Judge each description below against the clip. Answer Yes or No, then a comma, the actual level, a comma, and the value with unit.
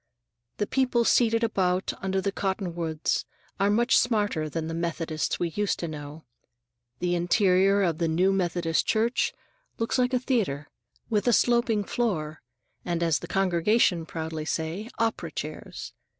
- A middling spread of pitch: Yes, average, 5.0 semitones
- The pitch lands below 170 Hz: No, medium, 185 Hz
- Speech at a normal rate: Yes, average, 150 wpm